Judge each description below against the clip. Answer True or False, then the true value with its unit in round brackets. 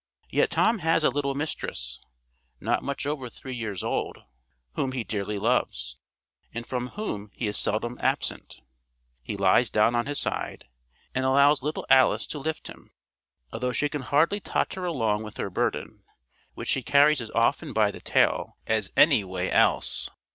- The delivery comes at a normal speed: True (170 wpm)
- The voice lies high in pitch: False (125 Hz)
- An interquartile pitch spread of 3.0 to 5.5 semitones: True (5.2 semitones)